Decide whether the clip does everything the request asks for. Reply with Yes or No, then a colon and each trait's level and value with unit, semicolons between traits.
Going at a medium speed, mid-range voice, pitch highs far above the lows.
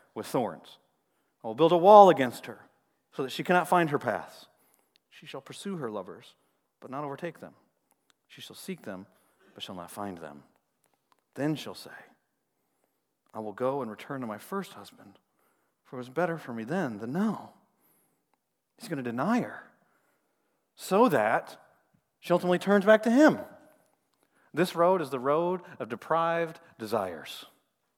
Yes: average, 165 wpm; medium, 165 Hz; wide, 6.3 semitones